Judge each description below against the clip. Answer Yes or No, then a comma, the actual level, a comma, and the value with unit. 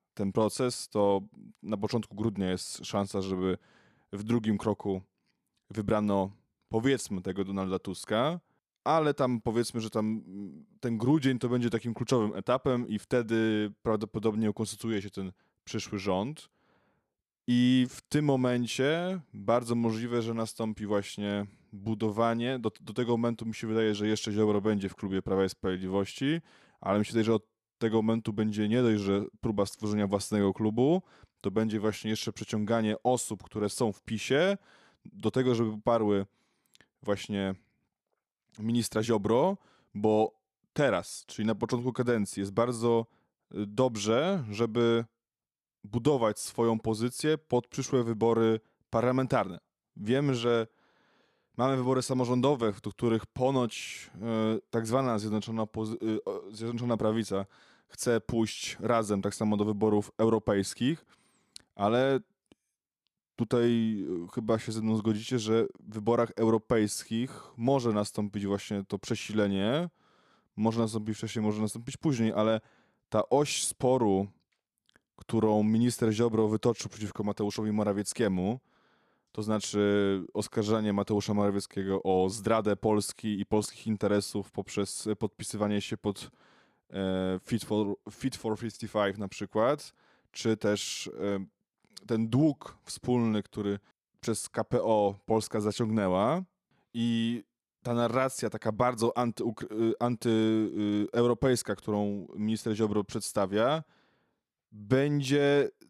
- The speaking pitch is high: No, low, 110 Hz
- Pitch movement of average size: No, narrow, 2.3 semitones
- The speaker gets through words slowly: No, average, 120 wpm